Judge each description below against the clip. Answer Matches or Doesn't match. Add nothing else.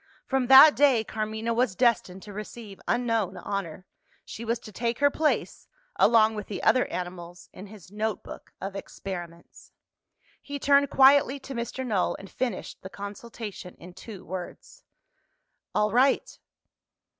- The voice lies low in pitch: Doesn't match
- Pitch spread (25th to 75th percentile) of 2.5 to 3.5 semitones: Doesn't match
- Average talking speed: Matches